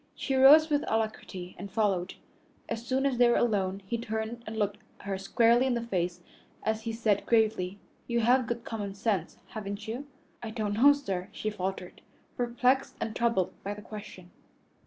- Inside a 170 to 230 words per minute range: Yes, average, 180 wpm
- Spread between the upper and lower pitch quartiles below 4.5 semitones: Yes, average, 3.1 semitones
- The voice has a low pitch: No, high, 220 Hz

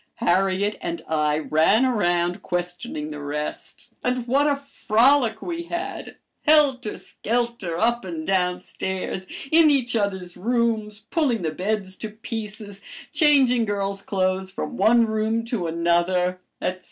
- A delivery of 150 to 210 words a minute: No, slow, 135 wpm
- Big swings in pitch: No, average, 5.0 semitones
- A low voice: No, high, 210 Hz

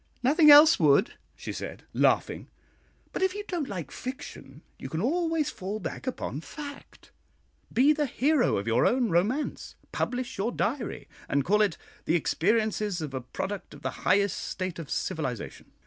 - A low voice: No, high, 215 Hz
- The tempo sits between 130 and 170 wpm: Yes, average, 165 wpm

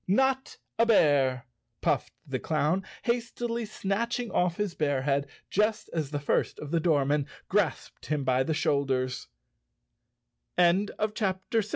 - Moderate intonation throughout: No, wide, 6.8 semitones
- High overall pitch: No, medium, 165 Hz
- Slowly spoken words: Yes, slow, 115 wpm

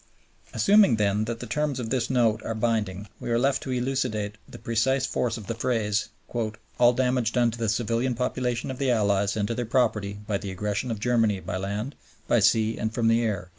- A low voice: Yes, low, 115 Hz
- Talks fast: Yes, fast, 210 wpm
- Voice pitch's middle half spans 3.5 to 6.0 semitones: No, average, 2.9 semitones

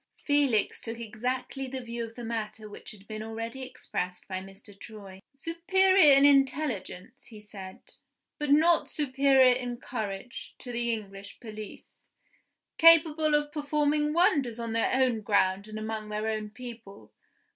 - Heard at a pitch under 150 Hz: No, high, 235 Hz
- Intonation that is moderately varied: Yes, average, 4.7 semitones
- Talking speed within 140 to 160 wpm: Yes, average, 145 wpm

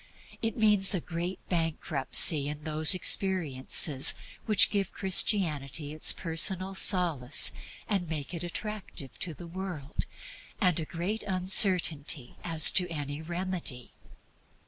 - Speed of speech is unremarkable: No, slow, 120 wpm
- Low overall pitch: No, medium, 170 Hz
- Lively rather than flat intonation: No, average, 3.9 semitones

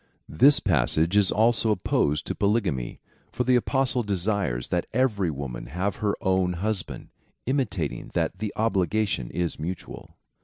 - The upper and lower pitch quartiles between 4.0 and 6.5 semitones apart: Yes, average, 4.5 semitones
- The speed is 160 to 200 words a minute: No, average, 150 wpm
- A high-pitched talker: No, low, 100 Hz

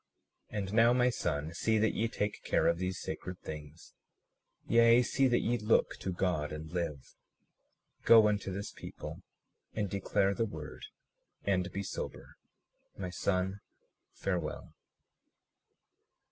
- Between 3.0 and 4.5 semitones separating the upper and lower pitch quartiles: Yes, average, 4.2 semitones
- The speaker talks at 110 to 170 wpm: Yes, slow, 135 wpm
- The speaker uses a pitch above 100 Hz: No, very low, 95 Hz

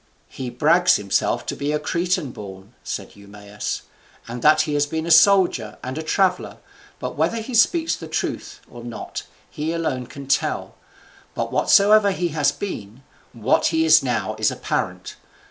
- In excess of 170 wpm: No, average, 165 wpm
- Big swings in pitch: Yes, wide, 6.8 semitones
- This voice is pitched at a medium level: Yes, medium, 150 Hz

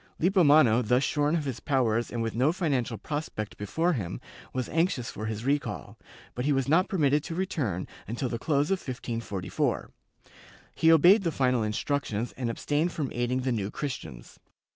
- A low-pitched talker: Yes, low, 130 Hz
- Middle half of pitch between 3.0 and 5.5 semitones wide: Yes, average, 5.0 semitones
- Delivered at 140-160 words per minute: No, average, 170 wpm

